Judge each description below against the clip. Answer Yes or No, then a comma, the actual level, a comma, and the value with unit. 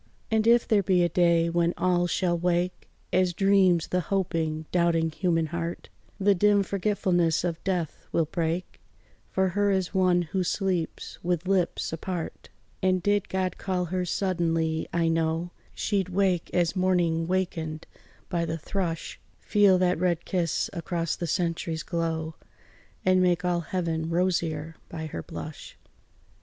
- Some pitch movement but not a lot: No, narrow, 2.1 semitones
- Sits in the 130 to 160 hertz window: No, medium, 175 Hz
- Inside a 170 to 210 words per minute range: No, average, 150 wpm